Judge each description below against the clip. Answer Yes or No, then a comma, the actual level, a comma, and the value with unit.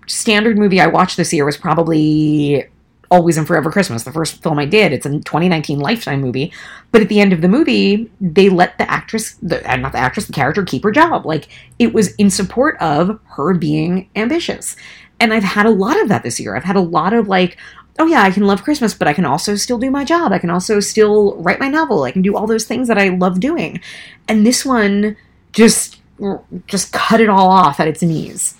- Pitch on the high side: Yes, high, 195 Hz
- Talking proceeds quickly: Yes, fast, 230 wpm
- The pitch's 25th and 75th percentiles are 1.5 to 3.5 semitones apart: No, average, 4.5 semitones